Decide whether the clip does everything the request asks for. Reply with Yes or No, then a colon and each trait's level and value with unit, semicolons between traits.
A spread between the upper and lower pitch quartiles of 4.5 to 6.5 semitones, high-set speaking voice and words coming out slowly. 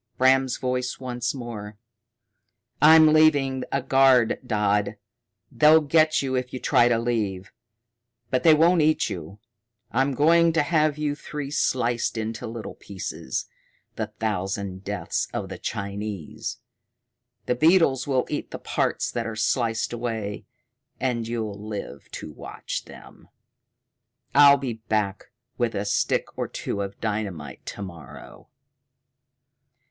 No: average, 4.8 semitones; low, 120 Hz; slow, 130 wpm